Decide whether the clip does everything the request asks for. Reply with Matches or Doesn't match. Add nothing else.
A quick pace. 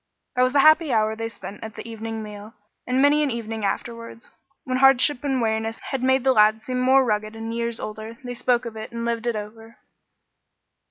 Matches